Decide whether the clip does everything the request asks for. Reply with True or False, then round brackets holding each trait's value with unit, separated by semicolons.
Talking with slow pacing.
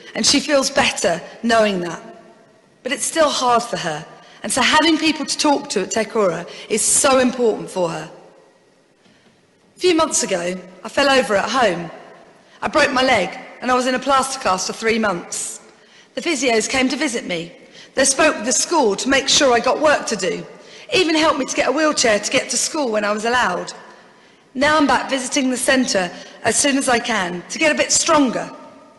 False (205 wpm)